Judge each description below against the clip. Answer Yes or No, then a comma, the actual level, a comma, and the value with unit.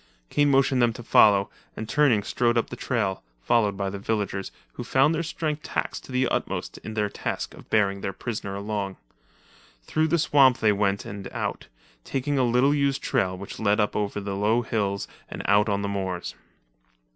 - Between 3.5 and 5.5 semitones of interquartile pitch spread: Yes, average, 4.5 semitones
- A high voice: No, low, 110 Hz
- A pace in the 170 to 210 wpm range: Yes, average, 190 wpm